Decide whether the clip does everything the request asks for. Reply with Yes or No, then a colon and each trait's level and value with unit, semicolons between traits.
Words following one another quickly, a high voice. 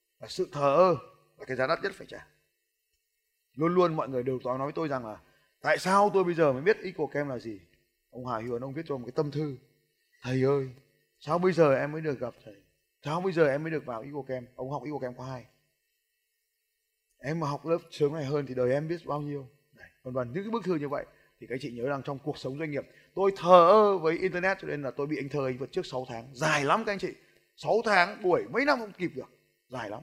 No: fast, 260 wpm; medium, 145 Hz